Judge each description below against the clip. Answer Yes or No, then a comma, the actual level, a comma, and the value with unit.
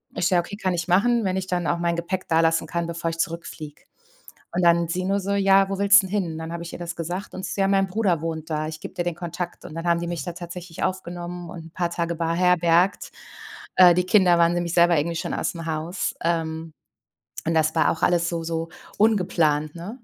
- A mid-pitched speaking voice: Yes, medium, 170 Hz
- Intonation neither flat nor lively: No, narrow, 1.8 semitones